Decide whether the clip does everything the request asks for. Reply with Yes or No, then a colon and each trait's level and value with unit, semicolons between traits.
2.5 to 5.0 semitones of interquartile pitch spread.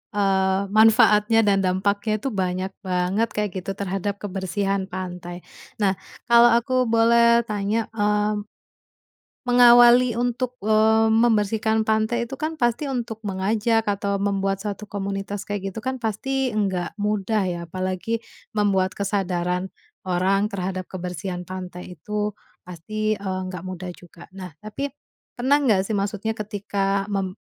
Yes: average, 2.8 semitones